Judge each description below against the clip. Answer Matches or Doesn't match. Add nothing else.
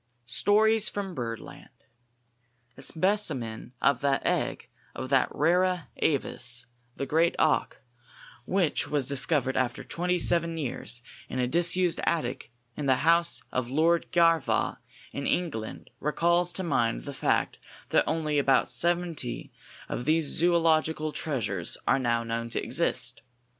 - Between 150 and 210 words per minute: Doesn't match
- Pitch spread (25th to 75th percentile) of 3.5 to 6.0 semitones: Matches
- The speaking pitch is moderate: Matches